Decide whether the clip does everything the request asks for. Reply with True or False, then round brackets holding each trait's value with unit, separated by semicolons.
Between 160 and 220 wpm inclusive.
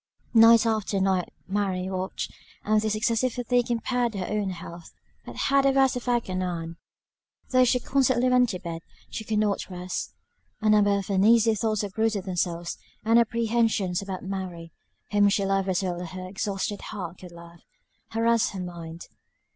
True (170 wpm)